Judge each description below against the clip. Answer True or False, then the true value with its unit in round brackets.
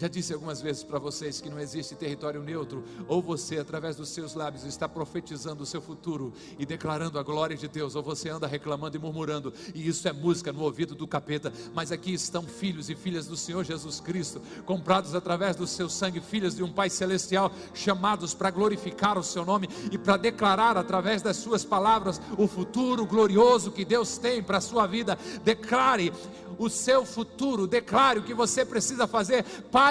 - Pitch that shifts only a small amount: False (5.0 semitones)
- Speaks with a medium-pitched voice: True (180 Hz)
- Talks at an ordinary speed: False (195 wpm)